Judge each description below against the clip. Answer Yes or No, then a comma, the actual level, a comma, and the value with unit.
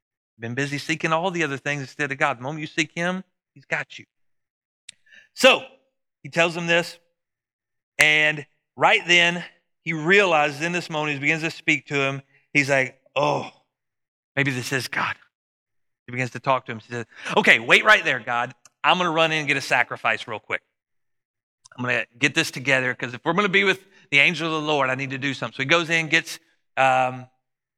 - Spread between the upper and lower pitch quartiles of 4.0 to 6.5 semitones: Yes, average, 4.3 semitones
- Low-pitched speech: No, medium, 150 Hz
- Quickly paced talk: Yes, fast, 210 wpm